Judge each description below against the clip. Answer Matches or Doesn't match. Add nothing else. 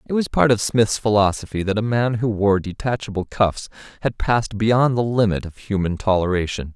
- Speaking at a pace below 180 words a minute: Doesn't match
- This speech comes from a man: Matches